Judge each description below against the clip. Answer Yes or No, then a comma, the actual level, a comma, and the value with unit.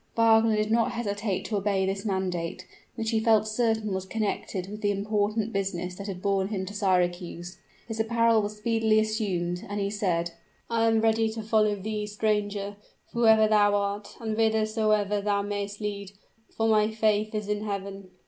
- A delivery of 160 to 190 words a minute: Yes, average, 175 wpm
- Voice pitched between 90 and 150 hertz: No, high, 210 Hz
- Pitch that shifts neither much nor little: No, narrow, 1.7 semitones